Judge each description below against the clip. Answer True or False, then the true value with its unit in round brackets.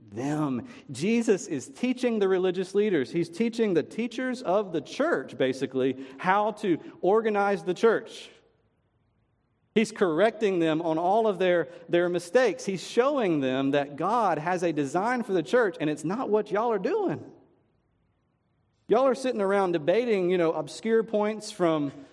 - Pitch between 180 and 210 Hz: True (190 Hz)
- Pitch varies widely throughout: True (5.9 semitones)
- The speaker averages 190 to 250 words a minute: False (155 wpm)